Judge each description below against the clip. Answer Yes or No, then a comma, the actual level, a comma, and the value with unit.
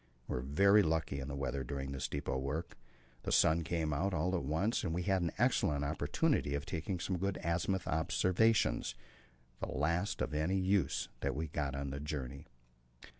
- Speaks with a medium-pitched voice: No, very low, 80 Hz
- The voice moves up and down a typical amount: Yes, average, 4.6 semitones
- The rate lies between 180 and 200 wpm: Yes, average, 185 wpm